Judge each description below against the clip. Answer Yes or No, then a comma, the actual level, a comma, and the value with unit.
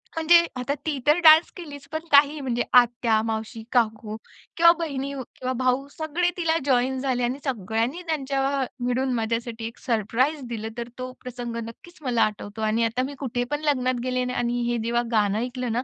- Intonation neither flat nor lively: Yes, average, 3.4 semitones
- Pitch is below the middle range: No, very high, 250 Hz